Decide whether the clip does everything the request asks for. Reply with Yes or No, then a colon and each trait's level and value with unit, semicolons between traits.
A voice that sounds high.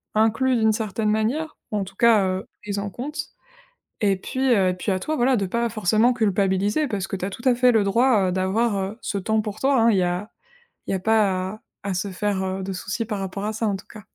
Yes: high, 210 Hz